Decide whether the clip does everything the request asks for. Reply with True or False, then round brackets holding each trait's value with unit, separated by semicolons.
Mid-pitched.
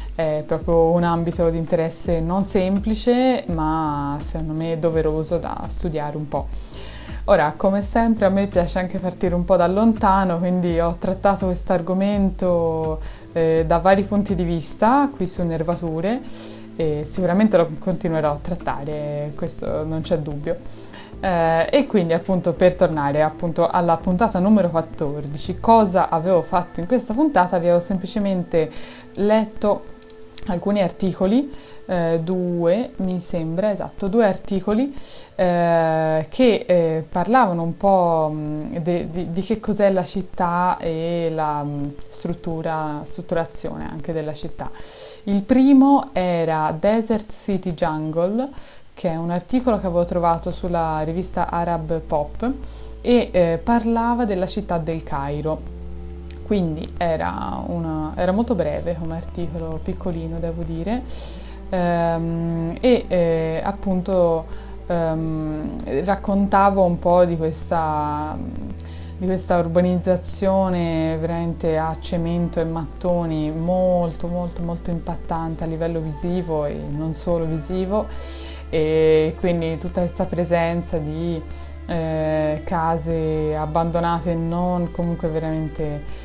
True (170 Hz)